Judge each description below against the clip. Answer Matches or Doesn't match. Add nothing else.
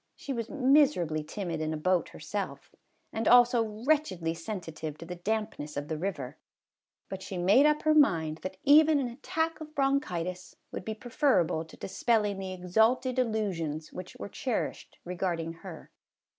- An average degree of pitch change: Doesn't match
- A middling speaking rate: Matches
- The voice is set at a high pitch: Matches